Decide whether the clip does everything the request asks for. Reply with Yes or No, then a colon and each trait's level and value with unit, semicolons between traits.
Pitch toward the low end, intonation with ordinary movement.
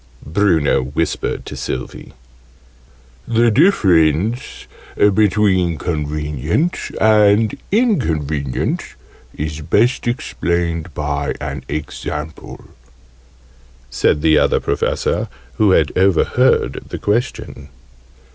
No: very low, 85 Hz; wide, 6.0 semitones